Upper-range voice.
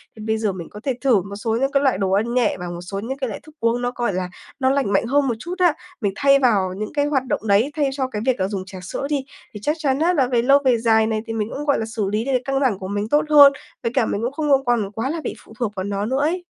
Yes: high, 235 Hz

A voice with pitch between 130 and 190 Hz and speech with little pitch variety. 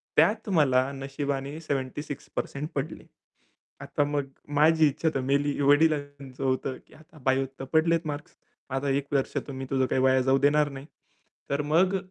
Yes: medium, 140 Hz; narrow, 2.1 semitones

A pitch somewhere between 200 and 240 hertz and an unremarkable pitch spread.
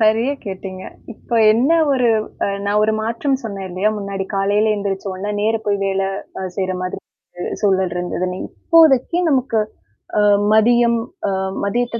Yes: high, 210 Hz; average, 3.5 semitones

